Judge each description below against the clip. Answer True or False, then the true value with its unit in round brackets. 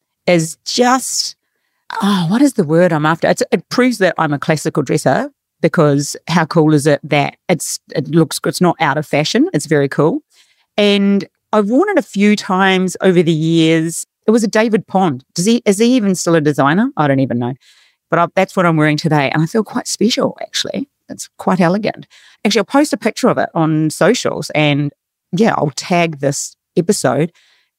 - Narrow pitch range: False (5.6 semitones)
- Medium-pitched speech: True (170 Hz)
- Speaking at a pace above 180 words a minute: True (200 wpm)